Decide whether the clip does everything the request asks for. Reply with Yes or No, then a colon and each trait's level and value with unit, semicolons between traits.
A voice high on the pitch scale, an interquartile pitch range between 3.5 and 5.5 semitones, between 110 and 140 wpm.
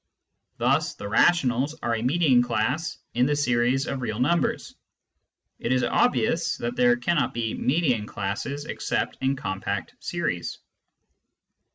No: low, 130 Hz; average, 4.9 semitones; slow, 135 wpm